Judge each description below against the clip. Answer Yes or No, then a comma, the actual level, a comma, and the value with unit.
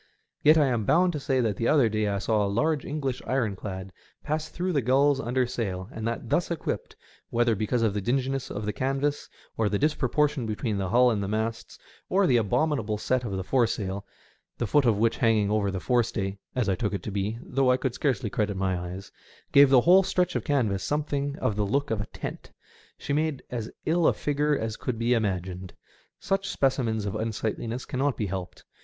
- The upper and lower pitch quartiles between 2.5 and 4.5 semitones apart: No, average, 5.1 semitones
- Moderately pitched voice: No, low, 115 Hz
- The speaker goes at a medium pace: No, fast, 215 wpm